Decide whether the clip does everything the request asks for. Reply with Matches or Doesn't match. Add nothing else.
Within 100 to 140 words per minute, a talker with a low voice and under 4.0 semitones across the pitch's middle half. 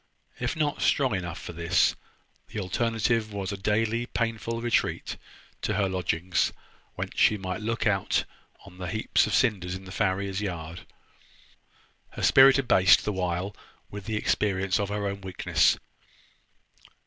Doesn't match